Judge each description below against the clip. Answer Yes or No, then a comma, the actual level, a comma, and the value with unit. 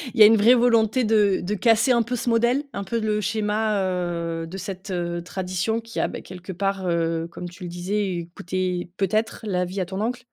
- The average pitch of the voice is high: Yes, high, 195 Hz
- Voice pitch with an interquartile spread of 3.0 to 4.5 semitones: Yes, average, 3.7 semitones